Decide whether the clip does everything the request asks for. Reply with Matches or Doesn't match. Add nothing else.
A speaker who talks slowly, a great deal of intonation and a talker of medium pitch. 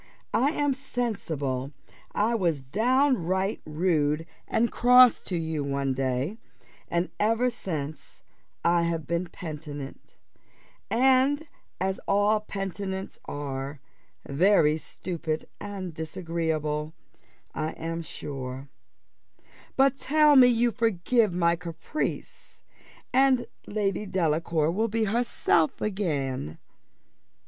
Matches